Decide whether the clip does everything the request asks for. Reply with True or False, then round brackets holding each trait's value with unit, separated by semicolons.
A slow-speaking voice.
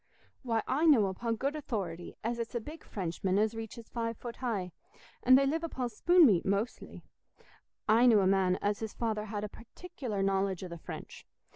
False (190 wpm)